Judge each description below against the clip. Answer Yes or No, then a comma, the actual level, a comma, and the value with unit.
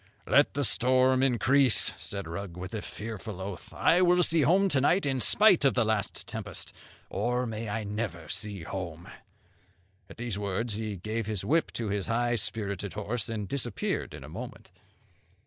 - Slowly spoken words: No, average, 175 wpm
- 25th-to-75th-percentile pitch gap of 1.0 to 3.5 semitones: No, average, 4.2 semitones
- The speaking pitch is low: Yes, low, 110 Hz